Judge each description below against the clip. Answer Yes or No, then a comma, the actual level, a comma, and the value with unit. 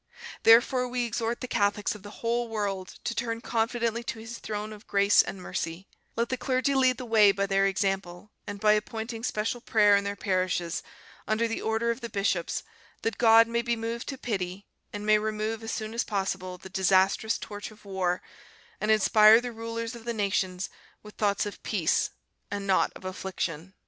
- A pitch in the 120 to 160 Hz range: No, high, 215 Hz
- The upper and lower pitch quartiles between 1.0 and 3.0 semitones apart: Yes, average, 2.7 semitones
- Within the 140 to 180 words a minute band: No, average, 190 wpm